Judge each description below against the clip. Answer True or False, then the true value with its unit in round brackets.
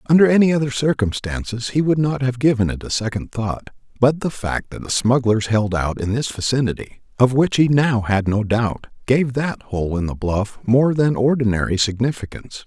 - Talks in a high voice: False (120 Hz)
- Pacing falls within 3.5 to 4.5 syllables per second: False (5.1 syllables/s)